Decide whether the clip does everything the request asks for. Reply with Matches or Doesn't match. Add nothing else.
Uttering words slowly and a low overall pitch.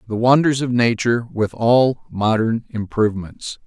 Matches